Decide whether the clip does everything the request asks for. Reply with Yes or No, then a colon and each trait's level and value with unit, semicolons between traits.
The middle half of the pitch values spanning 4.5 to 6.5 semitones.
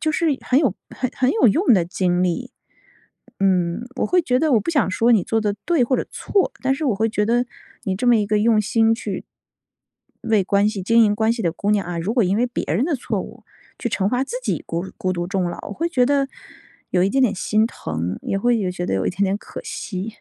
Yes: average, 4.8 semitones